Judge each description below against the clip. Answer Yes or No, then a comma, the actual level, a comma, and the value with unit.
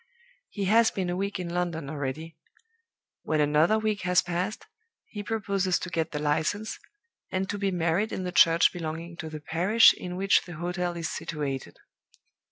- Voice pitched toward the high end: No, medium, 175 Hz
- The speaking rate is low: No, average, 175 wpm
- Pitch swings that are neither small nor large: Yes, average, 3.4 semitones